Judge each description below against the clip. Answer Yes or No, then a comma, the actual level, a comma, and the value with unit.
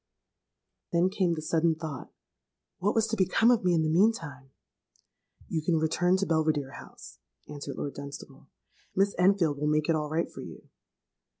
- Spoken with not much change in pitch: No, average, 3.6 semitones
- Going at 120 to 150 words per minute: No, average, 165 wpm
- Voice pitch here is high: No, medium, 165 Hz